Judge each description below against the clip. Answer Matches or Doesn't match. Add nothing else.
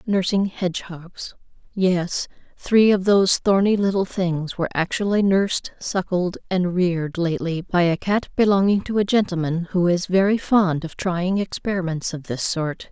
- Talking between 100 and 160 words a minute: Matches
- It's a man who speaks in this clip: Doesn't match